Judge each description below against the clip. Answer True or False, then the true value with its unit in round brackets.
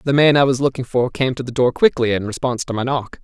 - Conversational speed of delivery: False (295 wpm)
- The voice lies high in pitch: False (130 Hz)